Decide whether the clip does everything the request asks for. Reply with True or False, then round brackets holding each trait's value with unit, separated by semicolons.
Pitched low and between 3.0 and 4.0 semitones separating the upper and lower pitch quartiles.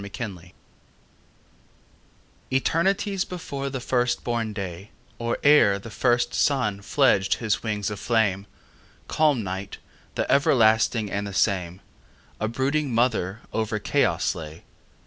False (110 Hz; 4.8 semitones)